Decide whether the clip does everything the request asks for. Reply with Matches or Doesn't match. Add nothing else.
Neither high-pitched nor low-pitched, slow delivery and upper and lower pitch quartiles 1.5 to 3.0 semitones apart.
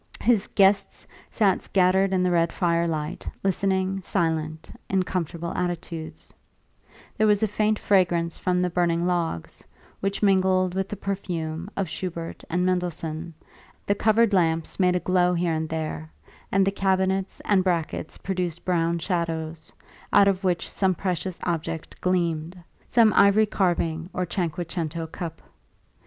Doesn't match